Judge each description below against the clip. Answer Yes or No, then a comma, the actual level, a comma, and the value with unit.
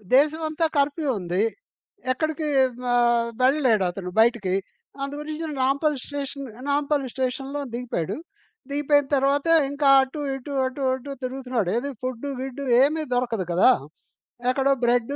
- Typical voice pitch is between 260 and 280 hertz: Yes, very high, 270 Hz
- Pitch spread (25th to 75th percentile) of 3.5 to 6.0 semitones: No, average, 2.9 semitones